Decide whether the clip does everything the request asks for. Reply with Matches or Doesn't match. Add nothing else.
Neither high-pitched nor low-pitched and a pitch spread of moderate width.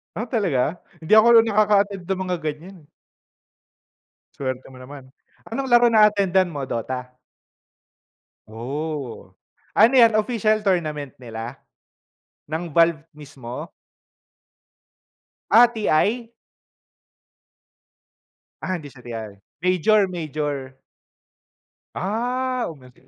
Doesn't match